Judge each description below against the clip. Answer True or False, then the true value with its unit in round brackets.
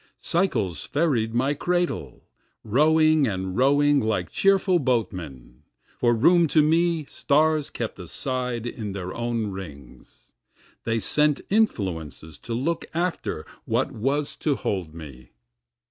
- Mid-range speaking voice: False (120 Hz)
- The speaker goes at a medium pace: False (120 wpm)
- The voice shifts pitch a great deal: True (8.2 semitones)